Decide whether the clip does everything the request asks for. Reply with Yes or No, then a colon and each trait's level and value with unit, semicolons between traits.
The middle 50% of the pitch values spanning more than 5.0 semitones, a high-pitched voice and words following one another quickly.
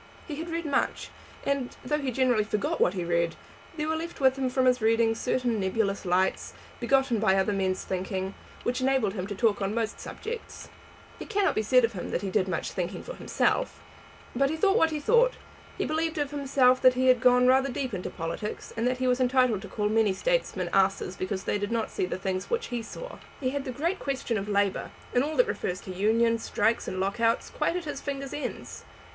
Yes: wide, 5.6 semitones; high, 240 Hz; fast, 225 wpm